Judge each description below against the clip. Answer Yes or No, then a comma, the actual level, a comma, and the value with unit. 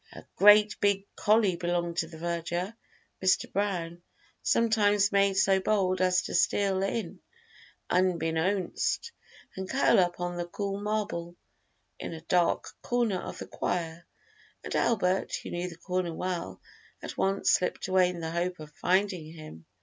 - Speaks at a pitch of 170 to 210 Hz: Yes, medium, 185 Hz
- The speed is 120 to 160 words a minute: Yes, average, 150 wpm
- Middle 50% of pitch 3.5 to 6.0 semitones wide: No, narrow, 2.6 semitones